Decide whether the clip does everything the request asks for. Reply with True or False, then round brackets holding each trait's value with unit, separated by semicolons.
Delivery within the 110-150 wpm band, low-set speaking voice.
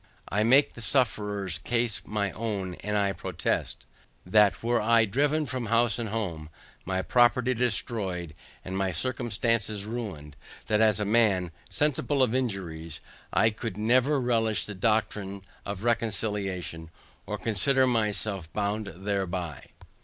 True (135 wpm; 105 Hz)